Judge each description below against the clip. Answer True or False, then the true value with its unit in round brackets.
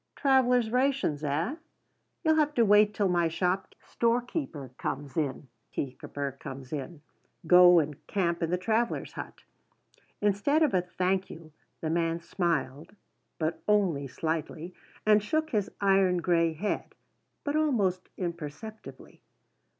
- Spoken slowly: True (120 wpm)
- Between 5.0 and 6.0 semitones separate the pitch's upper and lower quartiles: True (5.3 semitones)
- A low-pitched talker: False (180 Hz)